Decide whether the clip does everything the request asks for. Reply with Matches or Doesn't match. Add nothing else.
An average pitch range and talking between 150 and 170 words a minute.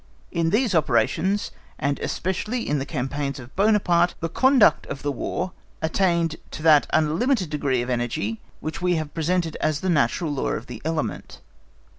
Matches